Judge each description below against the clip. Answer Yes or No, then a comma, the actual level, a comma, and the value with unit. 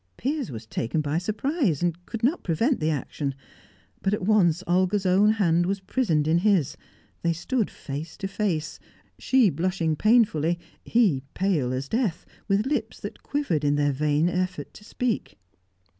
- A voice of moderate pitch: Yes, medium, 180 Hz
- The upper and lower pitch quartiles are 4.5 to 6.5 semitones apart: Yes, wide, 5.6 semitones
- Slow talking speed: No, average, 160 wpm